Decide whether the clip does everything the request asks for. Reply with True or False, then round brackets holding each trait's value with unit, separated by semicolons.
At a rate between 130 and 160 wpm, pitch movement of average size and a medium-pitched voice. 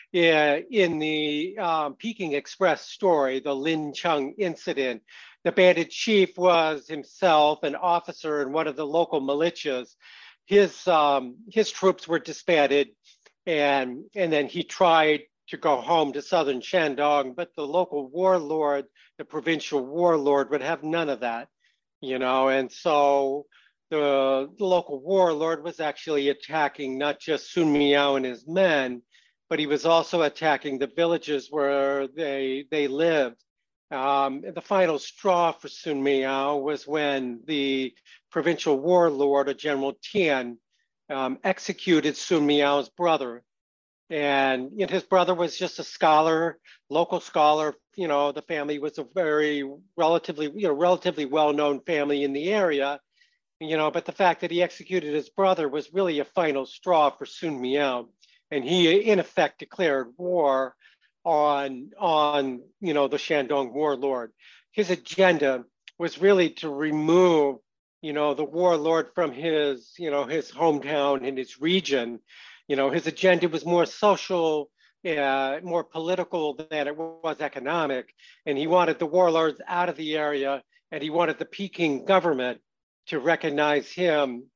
True (150 wpm; 3.4 semitones; 150 Hz)